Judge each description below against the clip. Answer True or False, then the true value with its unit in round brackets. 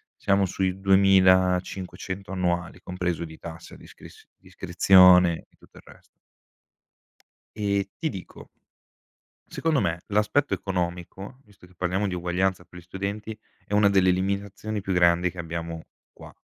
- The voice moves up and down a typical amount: False (1.9 semitones)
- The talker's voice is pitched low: True (95 Hz)